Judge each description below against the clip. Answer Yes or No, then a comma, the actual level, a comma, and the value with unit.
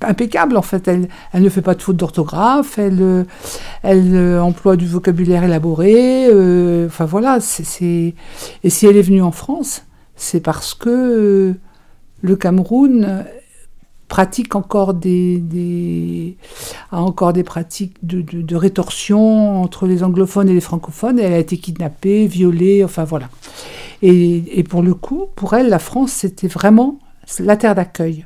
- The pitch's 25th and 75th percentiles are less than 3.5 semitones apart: Yes, average, 2.9 semitones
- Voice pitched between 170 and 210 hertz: Yes, medium, 185 Hz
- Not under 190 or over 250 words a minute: No, average, 160 wpm